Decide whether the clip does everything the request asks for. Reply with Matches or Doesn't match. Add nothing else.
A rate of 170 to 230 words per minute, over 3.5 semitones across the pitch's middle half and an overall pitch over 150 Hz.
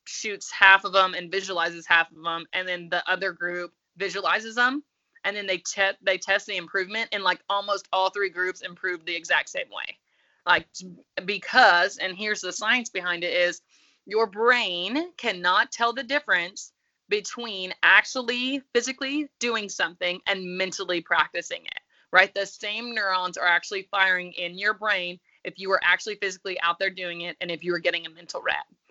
Matches